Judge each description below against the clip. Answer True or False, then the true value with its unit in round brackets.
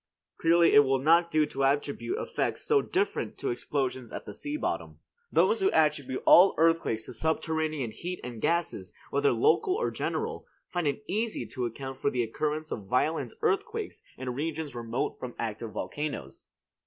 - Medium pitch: True (155 Hz)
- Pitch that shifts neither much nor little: False (5.8 semitones)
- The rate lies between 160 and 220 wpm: True (165 wpm)